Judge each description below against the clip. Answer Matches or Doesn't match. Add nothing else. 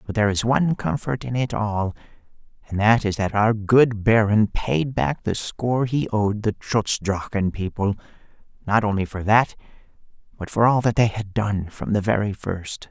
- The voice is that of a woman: Doesn't match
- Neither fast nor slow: Matches